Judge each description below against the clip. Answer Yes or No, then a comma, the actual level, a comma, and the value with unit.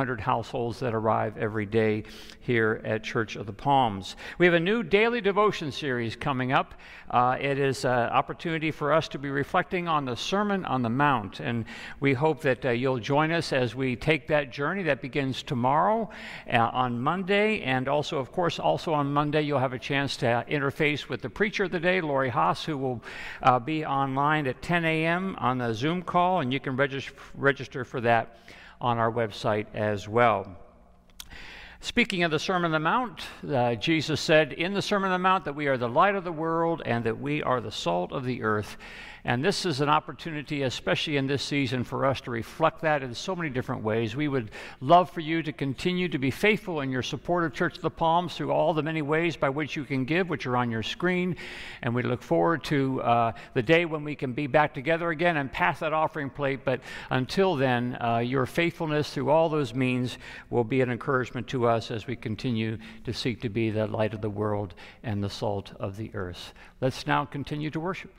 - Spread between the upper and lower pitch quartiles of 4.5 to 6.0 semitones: Yes, average, 5.1 semitones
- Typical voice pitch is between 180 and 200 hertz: No, medium, 140 Hz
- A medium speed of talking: No, fast, 215 wpm